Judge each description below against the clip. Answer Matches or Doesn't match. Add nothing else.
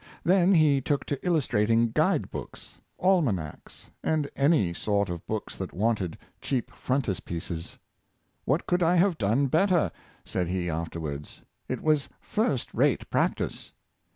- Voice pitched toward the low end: Matches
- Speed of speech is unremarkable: Doesn't match